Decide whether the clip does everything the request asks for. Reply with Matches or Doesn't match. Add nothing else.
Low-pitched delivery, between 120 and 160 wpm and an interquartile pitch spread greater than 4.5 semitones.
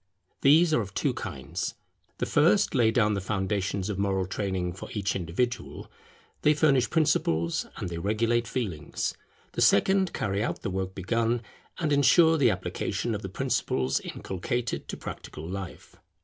Matches